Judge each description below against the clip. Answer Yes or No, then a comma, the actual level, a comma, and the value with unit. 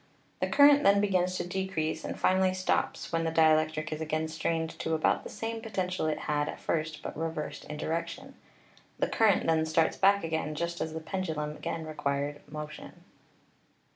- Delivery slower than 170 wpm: No, average, 180 wpm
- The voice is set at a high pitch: No, medium, 160 Hz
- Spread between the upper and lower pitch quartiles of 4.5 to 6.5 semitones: No, average, 3.1 semitones